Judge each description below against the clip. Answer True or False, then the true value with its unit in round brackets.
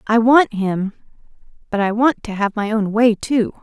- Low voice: False (220 Hz)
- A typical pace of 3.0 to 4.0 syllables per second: False (4.5 syllables/s)